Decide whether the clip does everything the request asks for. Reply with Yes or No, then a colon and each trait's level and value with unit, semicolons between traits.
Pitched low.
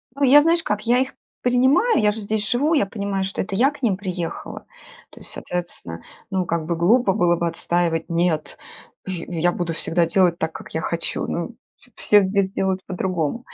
No: high, 190 Hz